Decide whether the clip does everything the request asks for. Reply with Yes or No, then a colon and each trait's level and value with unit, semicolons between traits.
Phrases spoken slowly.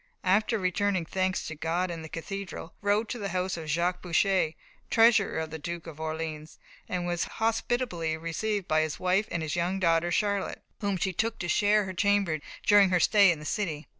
No: average, 200 wpm